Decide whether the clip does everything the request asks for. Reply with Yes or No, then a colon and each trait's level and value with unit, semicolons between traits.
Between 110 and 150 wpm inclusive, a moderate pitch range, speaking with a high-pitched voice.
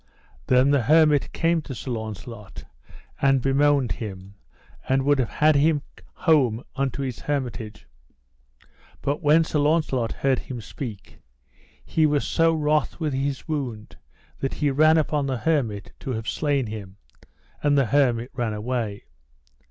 No: average, 145 wpm; average, 4.1 semitones; low, 135 Hz